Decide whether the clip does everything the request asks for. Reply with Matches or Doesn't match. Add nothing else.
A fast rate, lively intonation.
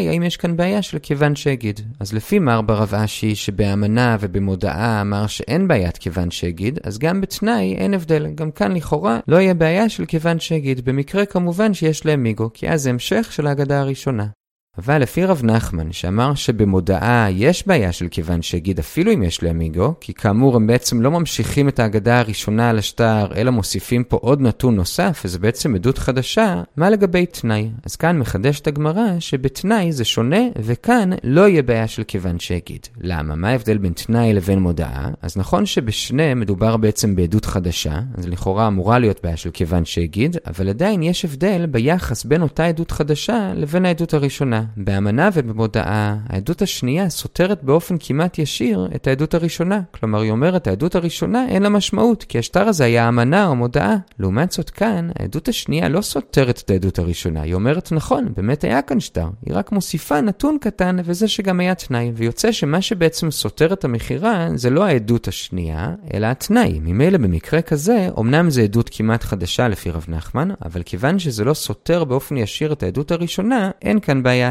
Matches